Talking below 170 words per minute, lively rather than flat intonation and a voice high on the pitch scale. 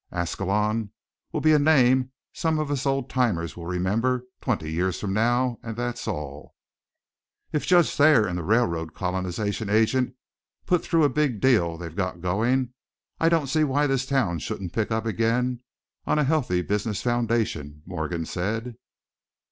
No: average, 160 wpm; wide, 6.2 semitones; low, 115 Hz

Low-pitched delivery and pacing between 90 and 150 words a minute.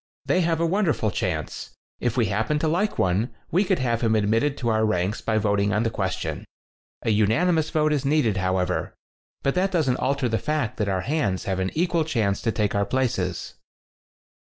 No: low, 115 Hz; average, 195 wpm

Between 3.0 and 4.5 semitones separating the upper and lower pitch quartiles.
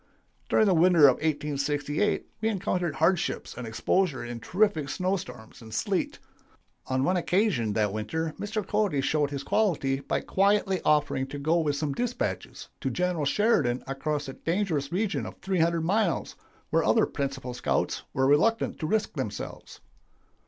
No: wide, 5.6 semitones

